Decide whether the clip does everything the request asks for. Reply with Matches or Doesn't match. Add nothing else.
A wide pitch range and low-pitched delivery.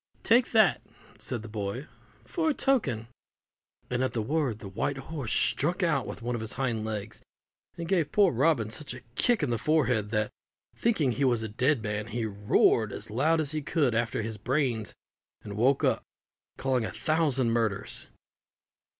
Matches